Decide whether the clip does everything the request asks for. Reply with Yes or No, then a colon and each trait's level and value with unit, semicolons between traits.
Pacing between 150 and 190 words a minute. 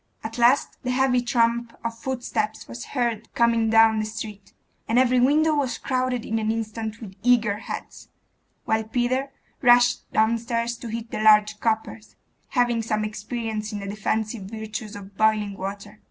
Yes: average, 160 wpm